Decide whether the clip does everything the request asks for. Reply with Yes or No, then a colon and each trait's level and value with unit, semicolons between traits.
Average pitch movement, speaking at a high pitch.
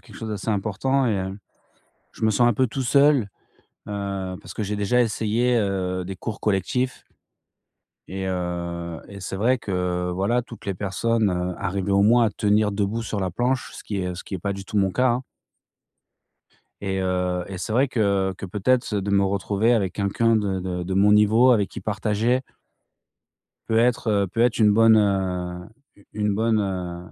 No: average, 3.1 semitones; low, 100 Hz